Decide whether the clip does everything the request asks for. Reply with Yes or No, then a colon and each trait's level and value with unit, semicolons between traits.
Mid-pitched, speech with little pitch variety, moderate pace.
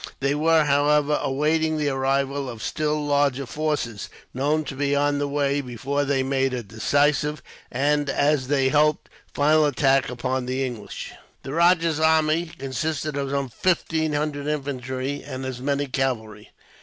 Yes: medium, 145 Hz; narrow, 2.1 semitones; average, 155 wpm